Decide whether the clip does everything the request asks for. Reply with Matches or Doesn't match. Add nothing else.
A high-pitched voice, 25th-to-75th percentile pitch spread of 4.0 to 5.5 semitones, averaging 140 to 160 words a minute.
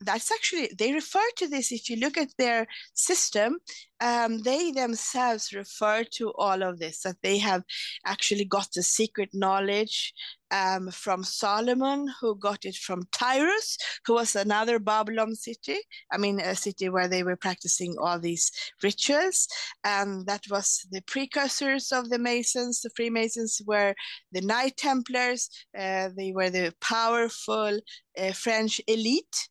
Matches